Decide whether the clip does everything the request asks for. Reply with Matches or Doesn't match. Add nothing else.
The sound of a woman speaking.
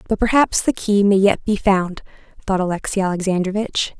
Matches